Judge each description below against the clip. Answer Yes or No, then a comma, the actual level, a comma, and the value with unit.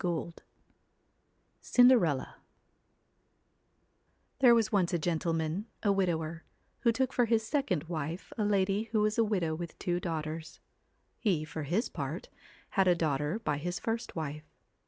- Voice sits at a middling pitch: Yes, medium, 175 Hz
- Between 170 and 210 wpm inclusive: No, average, 155 wpm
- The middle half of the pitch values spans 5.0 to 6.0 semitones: Yes, average, 5.3 semitones